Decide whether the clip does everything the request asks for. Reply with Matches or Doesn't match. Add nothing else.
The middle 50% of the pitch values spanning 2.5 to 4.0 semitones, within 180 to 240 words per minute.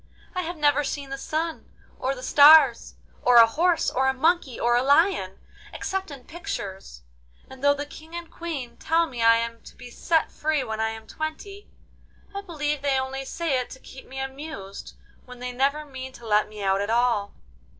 Doesn't match